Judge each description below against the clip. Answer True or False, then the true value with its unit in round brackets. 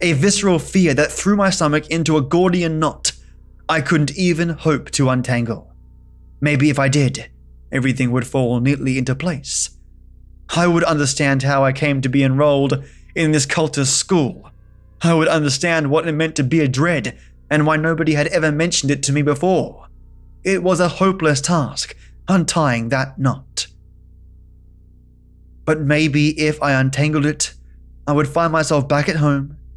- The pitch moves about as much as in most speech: True (4.7 semitones)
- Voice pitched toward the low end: False (145 Hz)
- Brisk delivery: False (165 wpm)